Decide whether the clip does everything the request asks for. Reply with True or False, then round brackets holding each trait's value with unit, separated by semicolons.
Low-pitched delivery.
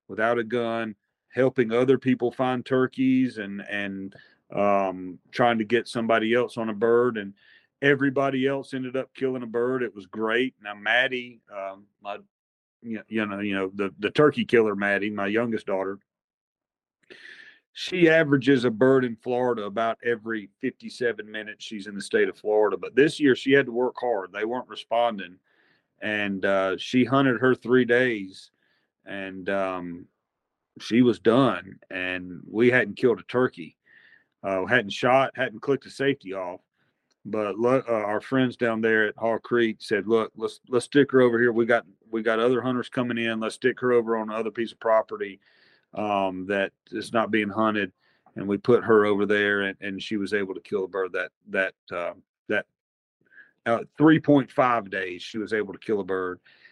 True (115 Hz)